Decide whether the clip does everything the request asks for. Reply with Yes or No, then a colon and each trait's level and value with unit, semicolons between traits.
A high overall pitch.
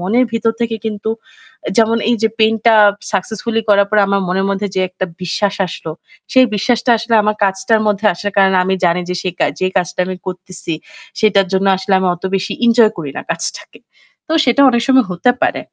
Yes: high, 205 Hz